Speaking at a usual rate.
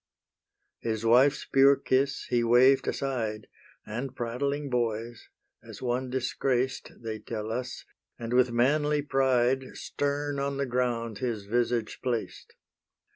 No: slow, 125 wpm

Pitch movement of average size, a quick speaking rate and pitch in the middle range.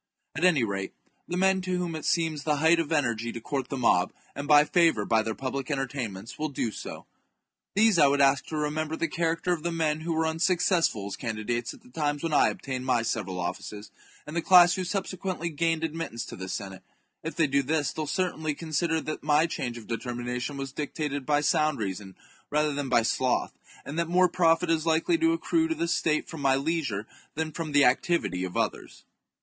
Yes: average, 5.0 semitones; fast, 215 wpm; medium, 150 Hz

